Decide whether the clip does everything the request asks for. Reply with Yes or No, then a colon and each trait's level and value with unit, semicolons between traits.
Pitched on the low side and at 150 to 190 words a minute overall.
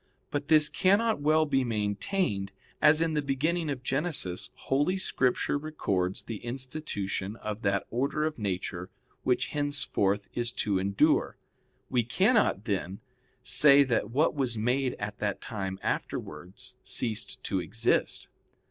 No: low, 125 Hz; slow, 135 wpm